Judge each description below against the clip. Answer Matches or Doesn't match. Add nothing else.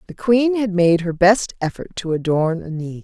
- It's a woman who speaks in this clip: Matches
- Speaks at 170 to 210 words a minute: Matches